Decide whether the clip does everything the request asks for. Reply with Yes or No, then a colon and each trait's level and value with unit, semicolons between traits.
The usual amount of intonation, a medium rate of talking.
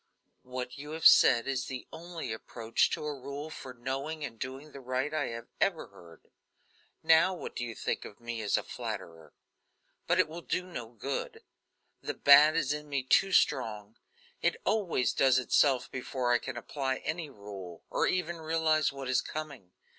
Yes: average, 4.4 semitones; average, 180 wpm